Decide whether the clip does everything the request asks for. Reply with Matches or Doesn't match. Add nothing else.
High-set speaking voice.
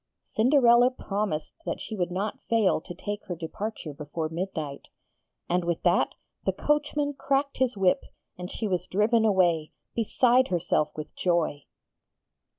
Matches